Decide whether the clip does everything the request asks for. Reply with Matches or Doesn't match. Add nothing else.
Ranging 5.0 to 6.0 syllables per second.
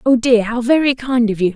Matches